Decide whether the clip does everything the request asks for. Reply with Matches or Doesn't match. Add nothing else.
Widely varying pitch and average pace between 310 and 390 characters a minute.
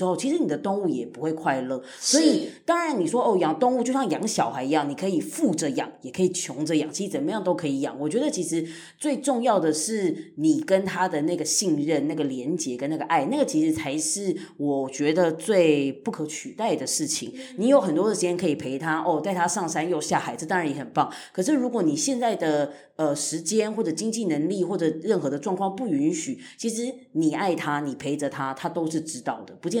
Matches